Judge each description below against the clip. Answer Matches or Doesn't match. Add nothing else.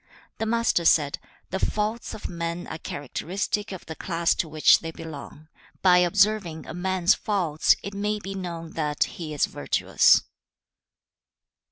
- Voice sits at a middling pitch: Matches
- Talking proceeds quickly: Doesn't match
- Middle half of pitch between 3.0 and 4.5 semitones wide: Matches